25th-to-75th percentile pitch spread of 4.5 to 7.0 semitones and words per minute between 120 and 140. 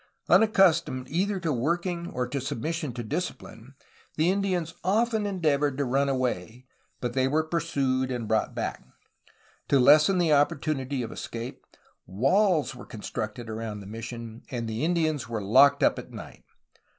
No: wide, 5.6 semitones; average, 150 wpm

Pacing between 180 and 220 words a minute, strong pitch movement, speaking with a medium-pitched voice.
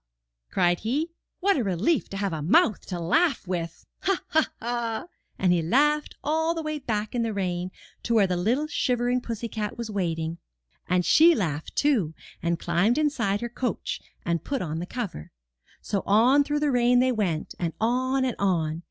No: average, 185 wpm; wide, 6.8 semitones; high, 225 Hz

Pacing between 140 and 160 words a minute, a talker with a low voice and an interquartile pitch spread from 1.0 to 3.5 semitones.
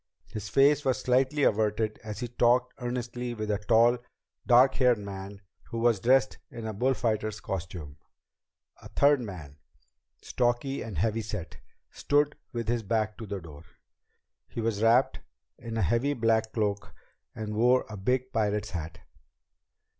Yes: average, 150 wpm; low, 115 Hz; average, 3.0 semitones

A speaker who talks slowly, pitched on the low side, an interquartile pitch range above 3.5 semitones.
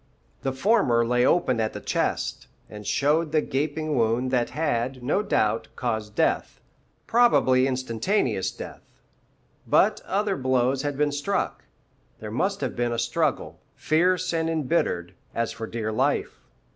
No: average, 145 wpm; low, 130 Hz; average, 5.3 semitones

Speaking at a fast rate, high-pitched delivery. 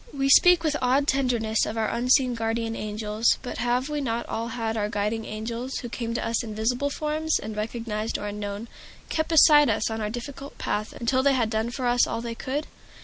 Yes: fast, 210 wpm; high, 235 Hz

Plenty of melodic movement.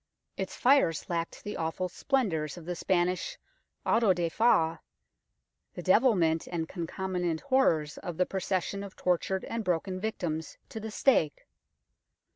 No: average, 3.8 semitones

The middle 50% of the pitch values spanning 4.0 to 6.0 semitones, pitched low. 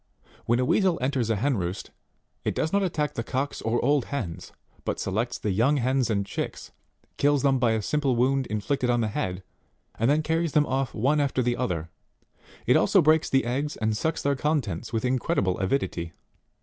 Yes: average, 4.6 semitones; low, 125 Hz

